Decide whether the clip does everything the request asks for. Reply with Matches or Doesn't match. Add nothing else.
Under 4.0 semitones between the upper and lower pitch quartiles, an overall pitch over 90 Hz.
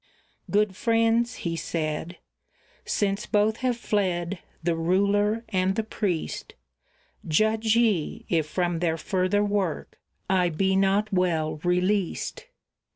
Matches